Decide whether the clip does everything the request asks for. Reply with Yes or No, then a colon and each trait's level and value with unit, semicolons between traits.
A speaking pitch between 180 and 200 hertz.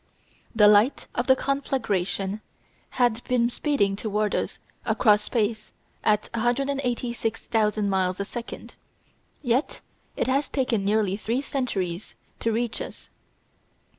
No: high, 225 Hz